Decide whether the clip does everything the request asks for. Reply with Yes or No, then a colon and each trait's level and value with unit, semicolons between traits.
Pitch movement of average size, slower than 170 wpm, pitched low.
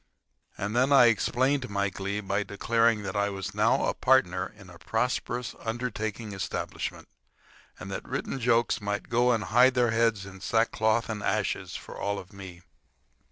Yes: average, 3.1 semitones; average, 160 wpm; low, 110 Hz